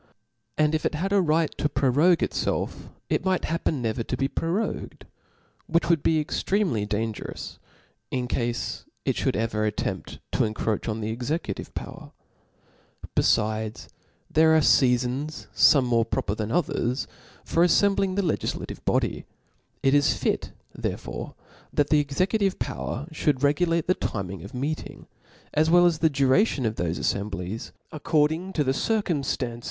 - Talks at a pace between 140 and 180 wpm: Yes, average, 150 wpm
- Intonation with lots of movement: Yes, wide, 6.1 semitones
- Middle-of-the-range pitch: Yes, medium, 145 Hz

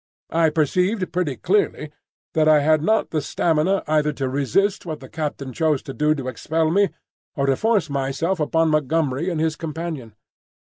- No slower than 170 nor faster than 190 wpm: Yes, average, 175 wpm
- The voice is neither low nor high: Yes, medium, 155 Hz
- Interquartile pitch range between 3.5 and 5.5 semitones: No, average, 2.9 semitones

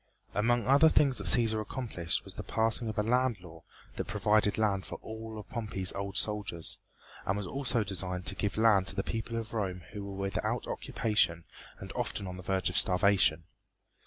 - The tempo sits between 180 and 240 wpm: Yes, average, 190 wpm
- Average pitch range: Yes, average, 3.1 semitones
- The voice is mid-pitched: No, low, 105 Hz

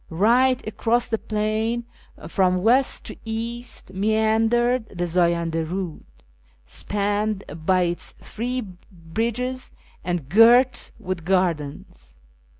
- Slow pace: Yes, slow, 100 wpm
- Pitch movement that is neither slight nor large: Yes, average, 4.9 semitones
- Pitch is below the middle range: No, high, 215 Hz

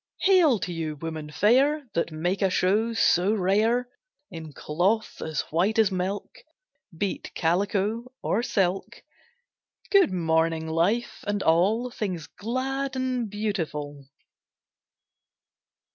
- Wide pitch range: Yes, wide, 5.8 semitones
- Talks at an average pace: No, slow, 115 wpm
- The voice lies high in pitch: Yes, high, 195 Hz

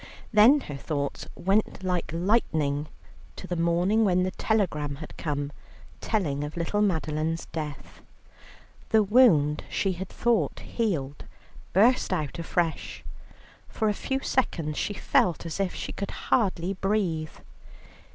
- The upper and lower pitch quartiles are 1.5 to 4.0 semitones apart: No, average, 5.2 semitones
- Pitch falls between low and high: Yes, medium, 175 Hz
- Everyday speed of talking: No, slow, 130 wpm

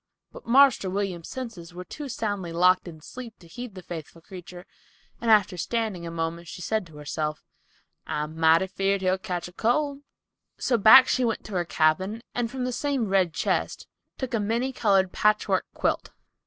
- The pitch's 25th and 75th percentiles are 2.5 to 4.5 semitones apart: No, average, 5.1 semitones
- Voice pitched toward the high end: Yes, high, 195 Hz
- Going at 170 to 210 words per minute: Yes, average, 180 wpm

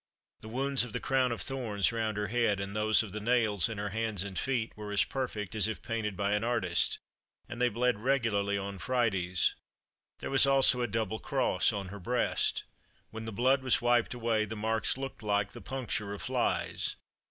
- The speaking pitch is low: Yes, low, 110 Hz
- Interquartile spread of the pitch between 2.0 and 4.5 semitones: Yes, average, 3.2 semitones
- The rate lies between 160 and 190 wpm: No, average, 200 wpm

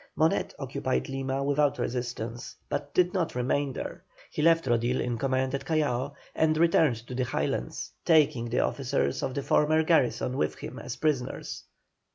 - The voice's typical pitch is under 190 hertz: Yes, low, 135 Hz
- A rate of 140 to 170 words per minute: Yes, average, 165 wpm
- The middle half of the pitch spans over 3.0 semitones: Yes, average, 3.8 semitones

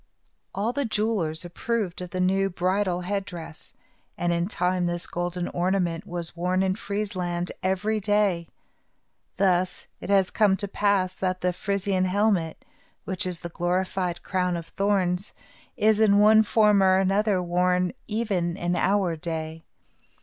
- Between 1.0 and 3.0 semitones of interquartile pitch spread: Yes, narrow, 2.4 semitones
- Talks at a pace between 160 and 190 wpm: No, average, 150 wpm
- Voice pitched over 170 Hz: Yes, medium, 185 Hz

